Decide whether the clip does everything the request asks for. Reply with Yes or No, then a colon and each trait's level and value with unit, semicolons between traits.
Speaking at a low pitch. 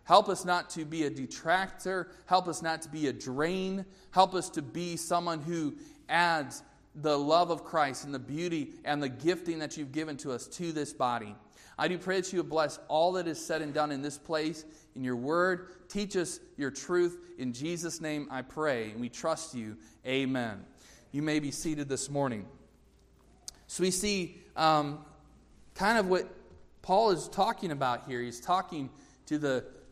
No: medium, 155 Hz